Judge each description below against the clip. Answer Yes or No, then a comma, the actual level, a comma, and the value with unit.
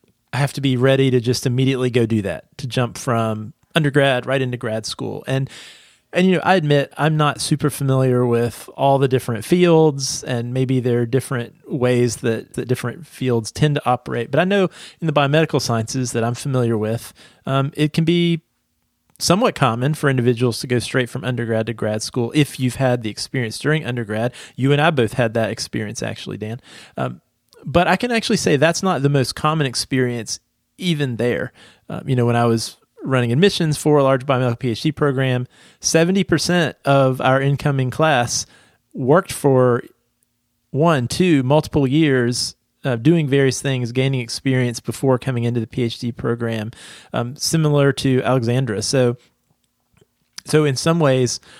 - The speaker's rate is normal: Yes, average, 175 wpm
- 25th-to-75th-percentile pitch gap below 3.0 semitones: No, average, 3.5 semitones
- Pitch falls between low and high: No, low, 130 Hz